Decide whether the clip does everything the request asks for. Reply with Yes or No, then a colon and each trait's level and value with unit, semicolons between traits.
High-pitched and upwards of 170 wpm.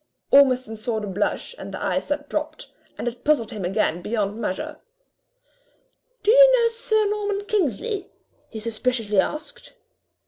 No: very high, 255 Hz; average, 145 wpm